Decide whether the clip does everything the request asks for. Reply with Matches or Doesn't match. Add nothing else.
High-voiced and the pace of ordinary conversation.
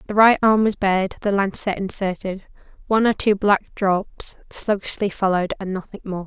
Matches